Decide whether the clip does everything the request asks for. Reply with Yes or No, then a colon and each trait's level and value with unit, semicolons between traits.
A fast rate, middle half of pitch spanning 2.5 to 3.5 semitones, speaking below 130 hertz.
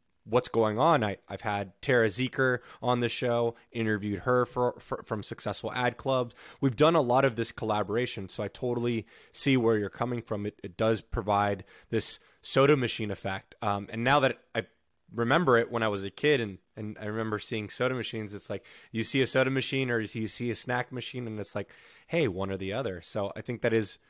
Yes: fast, 215 wpm; average, 3.0 semitones; low, 115 Hz